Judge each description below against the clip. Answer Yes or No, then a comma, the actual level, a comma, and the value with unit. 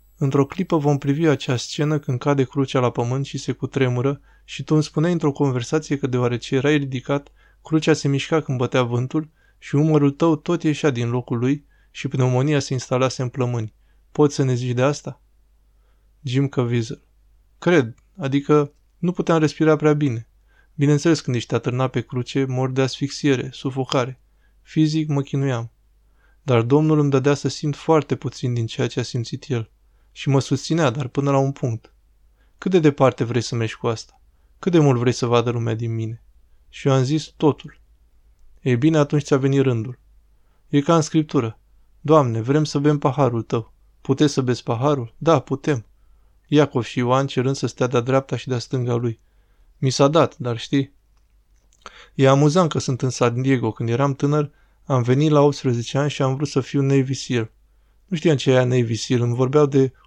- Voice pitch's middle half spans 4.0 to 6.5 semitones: No, average, 3.4 semitones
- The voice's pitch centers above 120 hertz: Yes, low, 135 Hz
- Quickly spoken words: Yes, fast, 185 wpm